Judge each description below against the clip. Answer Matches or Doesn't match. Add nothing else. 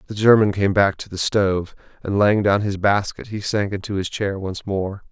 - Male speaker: Matches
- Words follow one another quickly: Matches